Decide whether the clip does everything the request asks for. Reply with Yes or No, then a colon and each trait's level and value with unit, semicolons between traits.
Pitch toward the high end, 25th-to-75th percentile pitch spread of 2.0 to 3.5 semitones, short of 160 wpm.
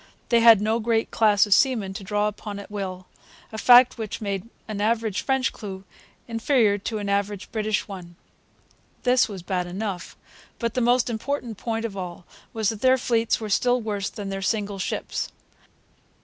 No: high, 215 Hz; average, 2.7 semitones; average, 175 wpm